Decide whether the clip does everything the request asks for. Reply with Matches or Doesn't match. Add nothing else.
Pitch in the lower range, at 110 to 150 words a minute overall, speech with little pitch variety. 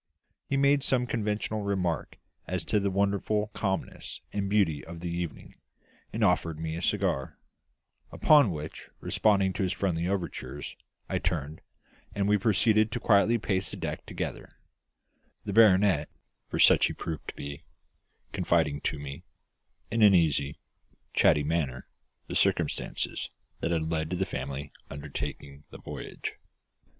Doesn't match